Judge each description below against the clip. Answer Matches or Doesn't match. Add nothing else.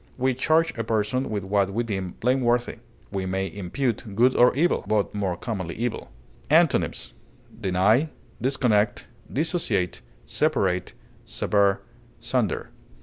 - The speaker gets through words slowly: Matches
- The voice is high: Doesn't match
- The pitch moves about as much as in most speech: Matches